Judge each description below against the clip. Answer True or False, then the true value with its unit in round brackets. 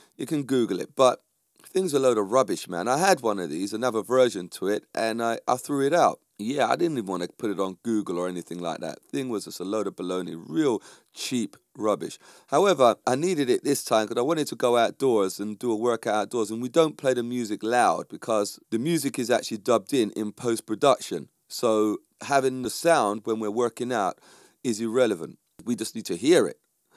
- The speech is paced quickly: True (225 wpm)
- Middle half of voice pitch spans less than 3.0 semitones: False (3.7 semitones)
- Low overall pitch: True (120 Hz)